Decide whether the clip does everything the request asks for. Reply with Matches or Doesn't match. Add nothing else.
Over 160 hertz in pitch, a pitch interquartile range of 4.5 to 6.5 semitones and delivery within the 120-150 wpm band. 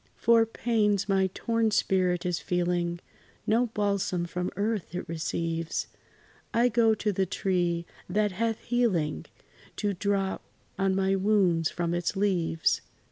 Doesn't match